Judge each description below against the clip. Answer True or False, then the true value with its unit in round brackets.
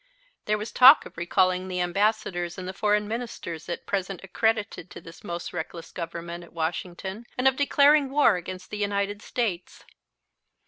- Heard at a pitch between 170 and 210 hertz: True (190 Hz)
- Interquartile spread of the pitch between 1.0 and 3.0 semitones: False (4.0 semitones)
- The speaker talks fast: False (165 wpm)